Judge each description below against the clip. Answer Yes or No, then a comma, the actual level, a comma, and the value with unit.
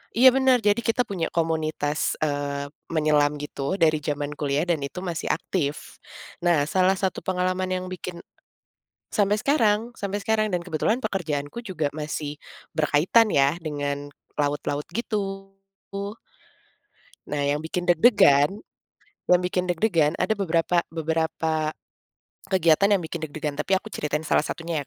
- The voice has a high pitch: No, medium, 165 Hz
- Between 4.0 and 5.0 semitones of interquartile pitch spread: Yes, average, 4.5 semitones